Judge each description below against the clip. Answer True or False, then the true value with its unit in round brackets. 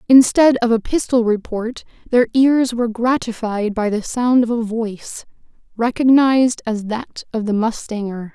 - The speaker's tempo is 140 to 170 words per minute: True (150 wpm)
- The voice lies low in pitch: False (230 Hz)